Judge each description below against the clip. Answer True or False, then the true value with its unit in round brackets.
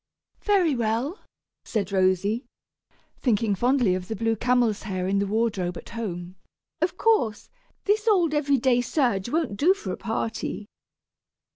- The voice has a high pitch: True (230 Hz)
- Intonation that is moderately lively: False (6.0 semitones)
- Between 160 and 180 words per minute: False (145 wpm)